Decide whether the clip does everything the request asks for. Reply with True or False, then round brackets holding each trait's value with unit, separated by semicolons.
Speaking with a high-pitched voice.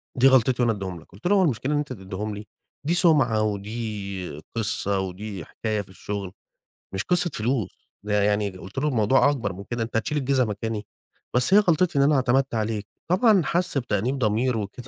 False (115 Hz)